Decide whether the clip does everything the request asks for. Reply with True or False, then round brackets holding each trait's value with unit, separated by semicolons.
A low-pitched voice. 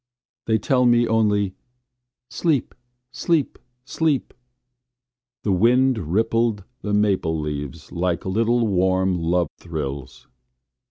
True (105 Hz)